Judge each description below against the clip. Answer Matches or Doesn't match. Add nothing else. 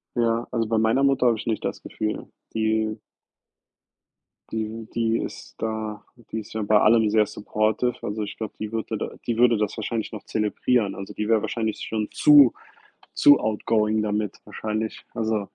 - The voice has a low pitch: Matches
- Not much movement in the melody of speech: Matches